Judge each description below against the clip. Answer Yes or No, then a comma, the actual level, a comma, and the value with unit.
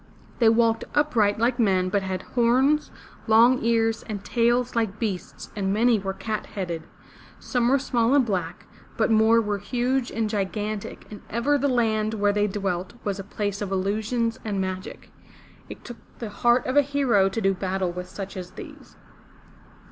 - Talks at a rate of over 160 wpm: Yes, average, 175 wpm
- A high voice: Yes, high, 220 Hz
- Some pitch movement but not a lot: Yes, average, 3.4 semitones